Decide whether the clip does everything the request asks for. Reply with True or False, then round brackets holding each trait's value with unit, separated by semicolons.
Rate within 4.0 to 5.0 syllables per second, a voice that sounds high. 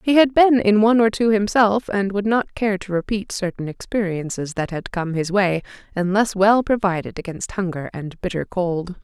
True (4.9 syllables/s; 200 Hz)